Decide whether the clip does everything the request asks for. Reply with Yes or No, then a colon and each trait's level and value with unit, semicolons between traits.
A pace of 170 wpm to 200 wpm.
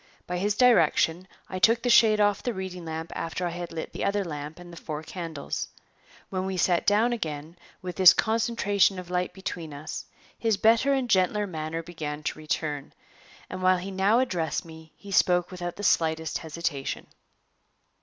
Yes: average, 180 wpm